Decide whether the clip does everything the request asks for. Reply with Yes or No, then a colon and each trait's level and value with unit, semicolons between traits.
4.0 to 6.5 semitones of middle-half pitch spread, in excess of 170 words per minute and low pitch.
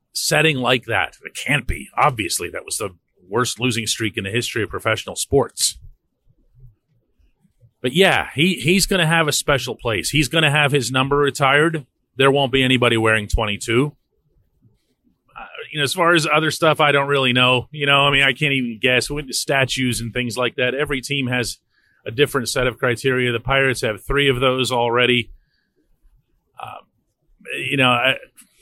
No: average, 2.9 semitones; average, 185 wpm; low, 130 Hz